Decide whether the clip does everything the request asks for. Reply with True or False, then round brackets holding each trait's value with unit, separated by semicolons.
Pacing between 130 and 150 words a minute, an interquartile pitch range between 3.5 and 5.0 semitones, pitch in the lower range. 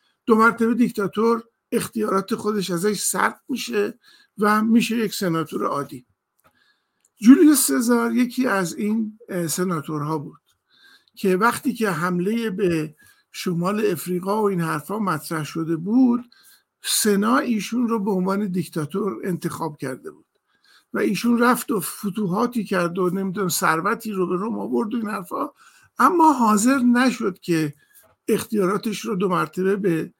False (135 wpm; 4.4 semitones; 210 Hz)